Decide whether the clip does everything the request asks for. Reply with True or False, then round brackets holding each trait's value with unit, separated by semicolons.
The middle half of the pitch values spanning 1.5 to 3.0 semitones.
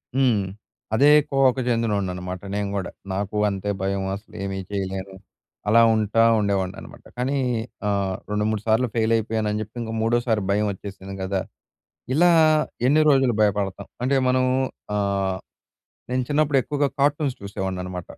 False (4.1 semitones)